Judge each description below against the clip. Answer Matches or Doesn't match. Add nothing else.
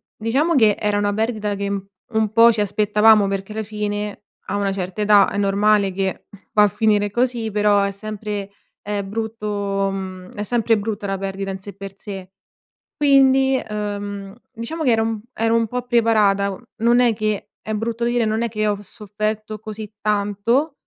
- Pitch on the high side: Matches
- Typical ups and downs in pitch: Doesn't match